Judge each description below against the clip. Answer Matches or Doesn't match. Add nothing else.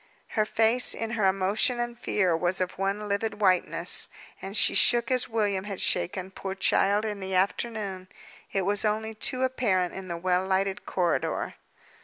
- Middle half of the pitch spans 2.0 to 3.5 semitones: Matches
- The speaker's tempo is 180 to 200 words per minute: Doesn't match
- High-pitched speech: Matches